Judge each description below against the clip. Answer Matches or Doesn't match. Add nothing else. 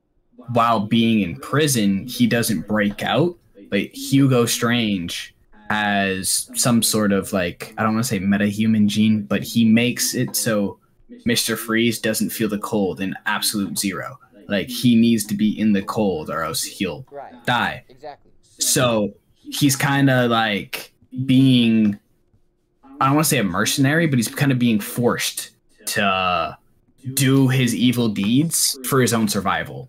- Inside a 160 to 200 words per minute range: Doesn't match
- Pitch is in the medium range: Doesn't match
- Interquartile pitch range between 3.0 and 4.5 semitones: Matches